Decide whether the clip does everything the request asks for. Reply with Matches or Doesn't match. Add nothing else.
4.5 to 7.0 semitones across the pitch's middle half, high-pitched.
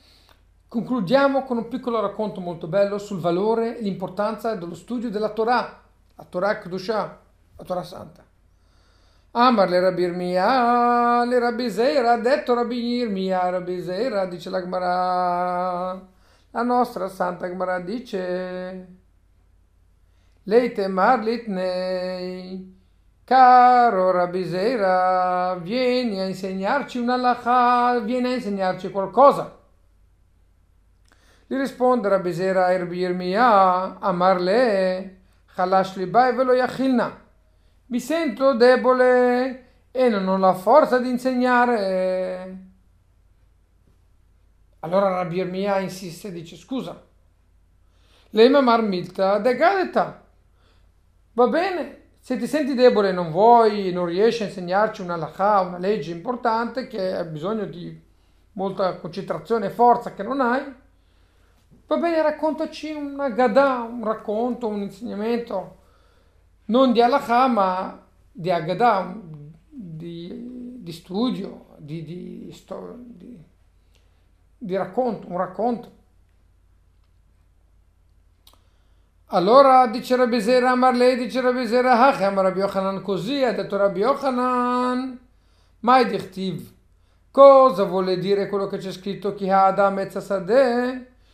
Matches